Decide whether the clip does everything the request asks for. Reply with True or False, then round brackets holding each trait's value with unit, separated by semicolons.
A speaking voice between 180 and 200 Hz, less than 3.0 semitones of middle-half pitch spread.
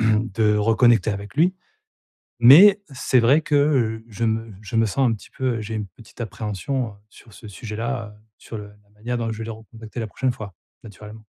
False (115 Hz; 2.5 semitones)